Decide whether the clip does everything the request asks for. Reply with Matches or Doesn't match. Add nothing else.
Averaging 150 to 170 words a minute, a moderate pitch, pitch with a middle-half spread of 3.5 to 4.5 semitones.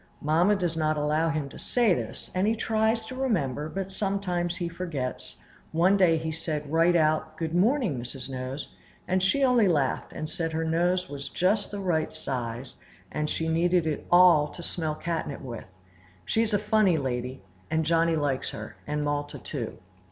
Doesn't match